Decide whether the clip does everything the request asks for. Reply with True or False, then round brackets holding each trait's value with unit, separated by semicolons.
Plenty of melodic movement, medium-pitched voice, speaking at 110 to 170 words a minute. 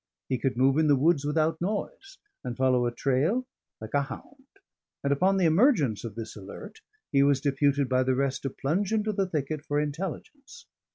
False (6.3 semitones; 145 Hz; 190 wpm)